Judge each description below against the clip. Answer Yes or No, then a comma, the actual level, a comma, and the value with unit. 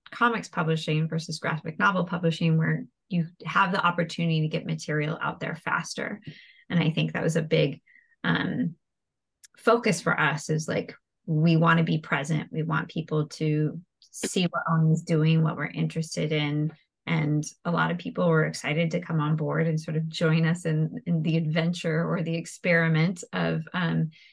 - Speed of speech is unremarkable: Yes, average, 180 wpm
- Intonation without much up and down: Yes, narrow, 1.4 semitones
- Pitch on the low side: No, medium, 165 Hz